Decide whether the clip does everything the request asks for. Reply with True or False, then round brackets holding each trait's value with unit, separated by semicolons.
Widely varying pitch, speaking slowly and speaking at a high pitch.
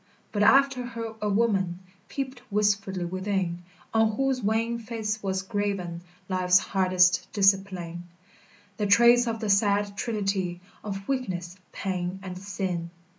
False (3.2 semitones; 125 wpm; 200 Hz)